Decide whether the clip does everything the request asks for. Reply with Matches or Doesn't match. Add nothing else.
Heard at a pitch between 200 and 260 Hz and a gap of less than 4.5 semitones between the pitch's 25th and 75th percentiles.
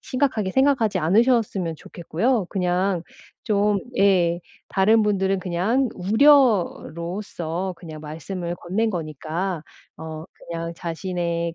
Doesn't match